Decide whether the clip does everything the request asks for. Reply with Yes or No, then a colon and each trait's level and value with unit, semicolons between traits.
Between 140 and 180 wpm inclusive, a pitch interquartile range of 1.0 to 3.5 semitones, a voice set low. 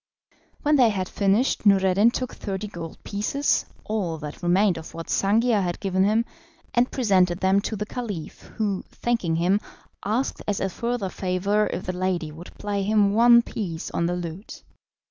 No: average, 170 wpm; average, 3.2 semitones; high, 200 Hz